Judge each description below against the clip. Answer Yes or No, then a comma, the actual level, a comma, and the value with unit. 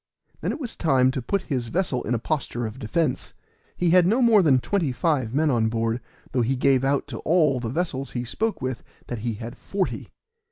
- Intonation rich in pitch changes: Yes, wide, 5.7 semitones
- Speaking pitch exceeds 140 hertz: No, low, 135 Hz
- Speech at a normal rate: No, fast, 215 wpm